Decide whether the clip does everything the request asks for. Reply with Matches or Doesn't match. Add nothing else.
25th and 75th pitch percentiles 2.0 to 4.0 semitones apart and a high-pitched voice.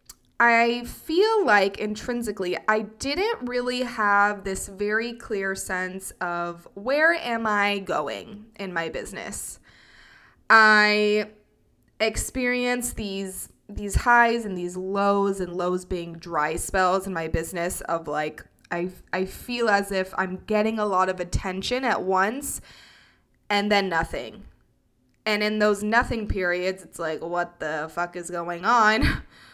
Matches